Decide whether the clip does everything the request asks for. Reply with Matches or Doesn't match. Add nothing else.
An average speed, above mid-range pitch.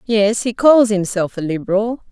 Matches